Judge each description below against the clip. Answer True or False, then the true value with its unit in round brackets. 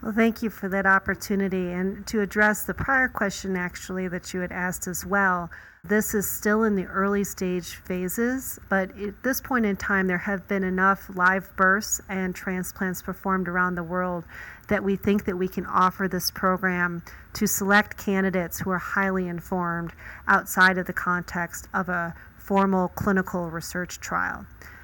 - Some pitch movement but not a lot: False (1.8 semitones)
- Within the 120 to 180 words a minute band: True (170 wpm)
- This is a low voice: False (190 Hz)